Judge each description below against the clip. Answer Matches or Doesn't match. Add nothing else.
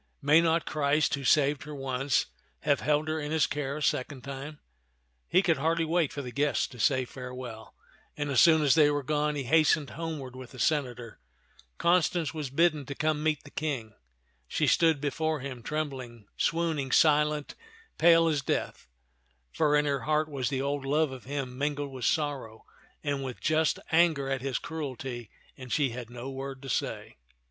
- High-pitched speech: Doesn't match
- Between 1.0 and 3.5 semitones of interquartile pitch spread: Matches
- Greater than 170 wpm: Matches